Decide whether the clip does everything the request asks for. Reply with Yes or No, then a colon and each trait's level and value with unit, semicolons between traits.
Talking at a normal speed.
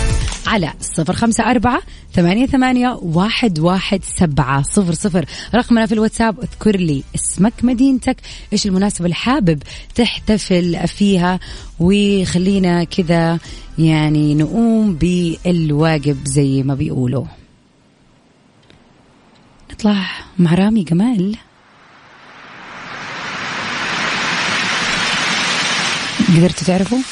No: slow, 85 wpm